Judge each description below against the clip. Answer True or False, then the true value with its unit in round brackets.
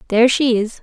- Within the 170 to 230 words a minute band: True (220 wpm)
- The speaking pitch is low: False (235 Hz)